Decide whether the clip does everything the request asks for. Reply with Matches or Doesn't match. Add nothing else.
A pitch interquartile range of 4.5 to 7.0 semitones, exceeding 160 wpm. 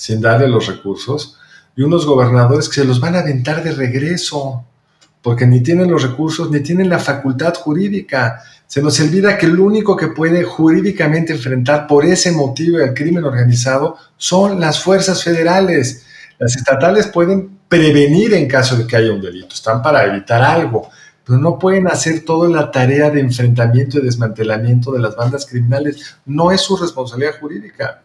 Matches